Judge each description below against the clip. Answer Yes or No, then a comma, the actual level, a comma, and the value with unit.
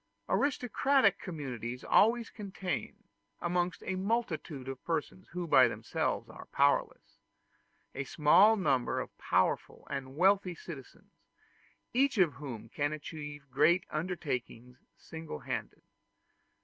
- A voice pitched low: No, medium, 165 Hz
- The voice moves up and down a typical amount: No, wide, 5.7 semitones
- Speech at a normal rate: No, slow, 110 wpm